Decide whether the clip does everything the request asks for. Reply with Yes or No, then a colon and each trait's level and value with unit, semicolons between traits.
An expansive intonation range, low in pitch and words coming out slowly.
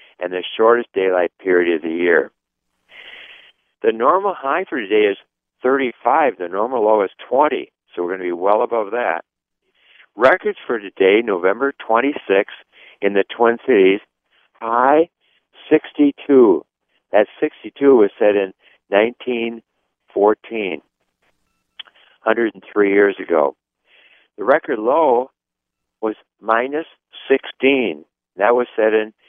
Yes: wide, 6.2 semitones; low, 110 Hz; slow, 120 wpm